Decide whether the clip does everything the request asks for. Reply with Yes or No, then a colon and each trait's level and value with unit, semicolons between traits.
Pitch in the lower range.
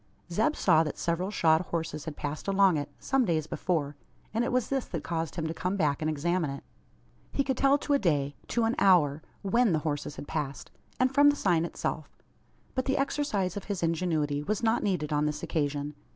No: medium, 170 Hz